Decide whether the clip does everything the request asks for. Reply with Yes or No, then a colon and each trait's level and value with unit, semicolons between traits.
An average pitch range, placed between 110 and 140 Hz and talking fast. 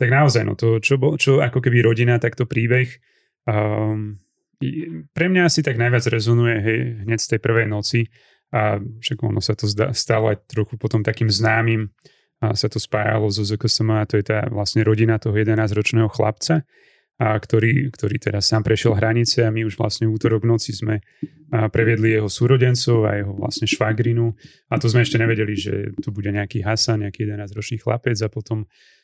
No: narrow, 1.9 semitones; low, 115 Hz; fast, 180 wpm